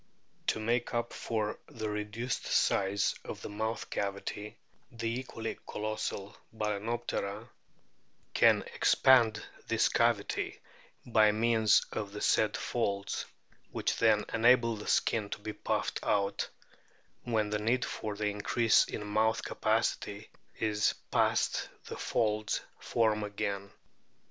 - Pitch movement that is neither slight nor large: No, narrow, 1.8 semitones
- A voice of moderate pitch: No, low, 110 Hz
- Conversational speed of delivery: No, slow, 120 wpm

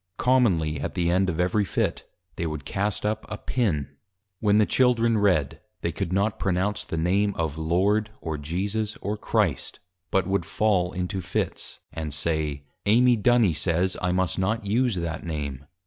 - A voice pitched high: No, very low, 95 Hz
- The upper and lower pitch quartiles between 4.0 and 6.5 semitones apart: Yes, average, 4.5 semitones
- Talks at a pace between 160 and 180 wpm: Yes, average, 170 wpm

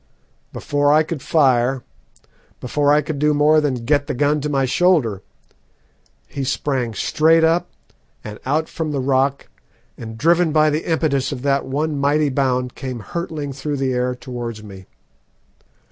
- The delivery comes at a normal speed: Yes, average, 160 wpm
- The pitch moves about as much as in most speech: Yes, average, 3.1 semitones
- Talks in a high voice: No, medium, 140 Hz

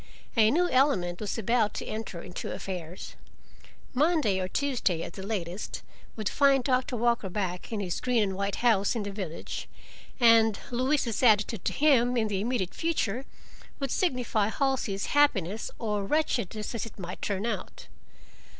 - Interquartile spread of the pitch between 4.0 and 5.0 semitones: Yes, average, 4.5 semitones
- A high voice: Yes, high, 220 Hz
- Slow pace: No, average, 160 wpm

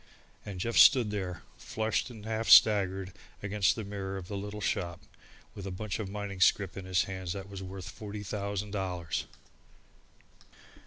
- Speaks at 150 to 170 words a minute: Yes, average, 165 wpm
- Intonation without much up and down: Yes, narrow, 1.9 semitones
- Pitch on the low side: Yes, low, 100 Hz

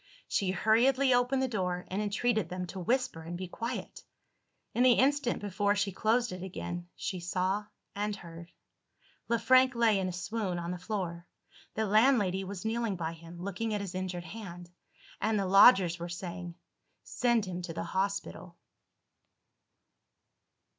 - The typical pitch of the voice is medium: No, high, 195 Hz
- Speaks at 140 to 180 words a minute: Yes, average, 160 wpm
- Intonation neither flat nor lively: Yes, average, 4.1 semitones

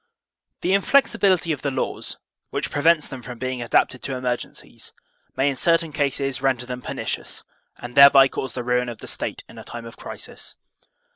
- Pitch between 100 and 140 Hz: Yes, low, 135 Hz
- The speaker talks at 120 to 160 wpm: No, average, 185 wpm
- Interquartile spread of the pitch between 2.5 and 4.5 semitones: Yes, average, 3.0 semitones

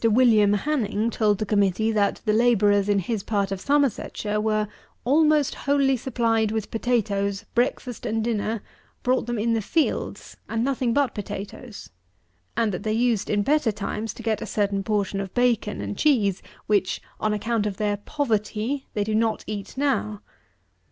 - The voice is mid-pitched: No, high, 220 Hz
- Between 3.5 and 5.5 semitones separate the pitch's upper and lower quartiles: No, average, 2.8 semitones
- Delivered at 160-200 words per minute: Yes, average, 165 wpm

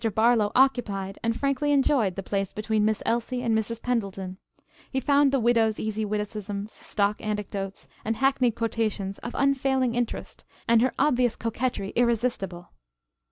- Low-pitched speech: No, high, 225 Hz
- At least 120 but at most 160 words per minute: Yes, average, 145 wpm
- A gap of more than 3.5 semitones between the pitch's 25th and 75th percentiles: No, average, 3.2 semitones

